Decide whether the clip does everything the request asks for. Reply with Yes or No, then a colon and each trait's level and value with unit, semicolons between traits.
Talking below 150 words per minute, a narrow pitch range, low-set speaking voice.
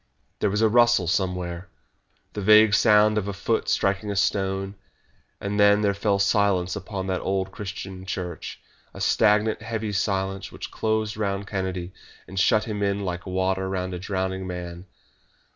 No: average, 160 wpm; narrow, 1.9 semitones; low, 100 Hz